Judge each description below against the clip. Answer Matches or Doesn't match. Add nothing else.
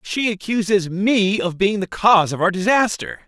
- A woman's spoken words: Doesn't match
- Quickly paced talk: Doesn't match